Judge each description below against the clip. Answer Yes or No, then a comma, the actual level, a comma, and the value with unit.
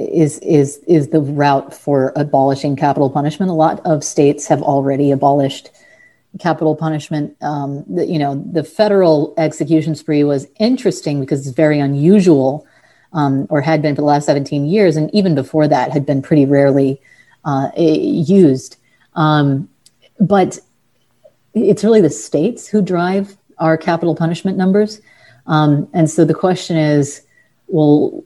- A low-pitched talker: No, medium, 155 Hz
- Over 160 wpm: No, average, 150 wpm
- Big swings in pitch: No, average, 3.2 semitones